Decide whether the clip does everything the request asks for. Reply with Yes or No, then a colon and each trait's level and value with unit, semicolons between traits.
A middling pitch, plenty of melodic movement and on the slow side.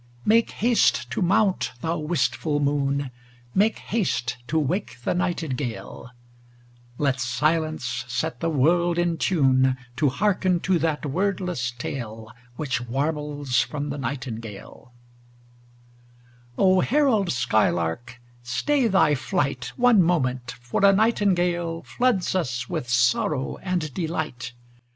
Yes: medium, 150 Hz; wide, 6.2 semitones; slow, 115 wpm